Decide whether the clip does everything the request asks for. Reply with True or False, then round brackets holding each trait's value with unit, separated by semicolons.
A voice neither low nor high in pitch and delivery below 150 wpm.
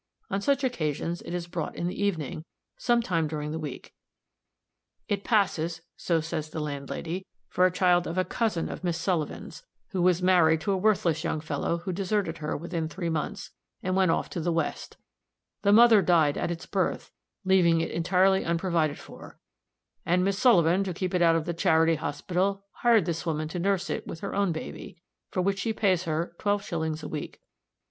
False (175 Hz; 195 wpm)